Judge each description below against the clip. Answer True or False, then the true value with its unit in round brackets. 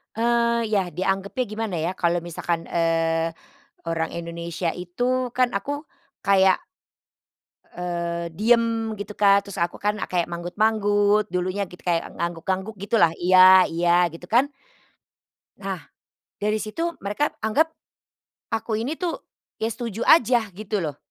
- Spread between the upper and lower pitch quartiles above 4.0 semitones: True (4.5 semitones)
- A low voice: False (200 Hz)